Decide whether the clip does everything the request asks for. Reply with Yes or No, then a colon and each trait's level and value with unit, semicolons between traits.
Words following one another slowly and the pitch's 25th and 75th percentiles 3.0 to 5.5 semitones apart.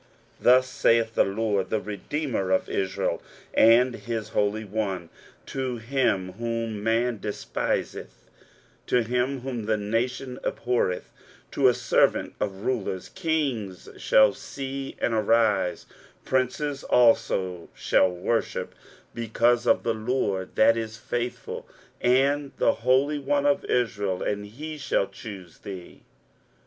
Yes: slow, 125 wpm; average, 3.8 semitones